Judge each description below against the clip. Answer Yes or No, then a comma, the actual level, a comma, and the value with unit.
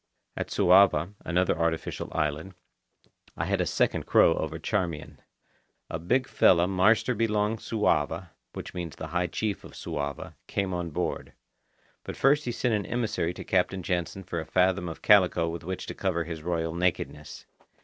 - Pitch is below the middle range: Yes, very low, 90 Hz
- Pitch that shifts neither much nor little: Yes, average, 3.4 semitones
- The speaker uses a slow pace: No, average, 165 wpm